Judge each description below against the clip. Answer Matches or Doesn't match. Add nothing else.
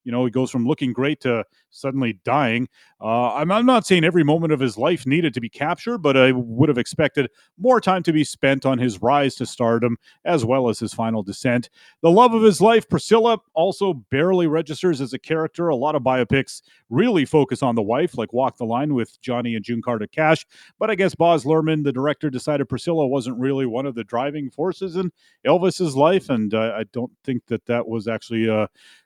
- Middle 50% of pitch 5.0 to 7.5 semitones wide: Matches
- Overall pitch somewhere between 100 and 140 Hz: Matches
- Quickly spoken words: Matches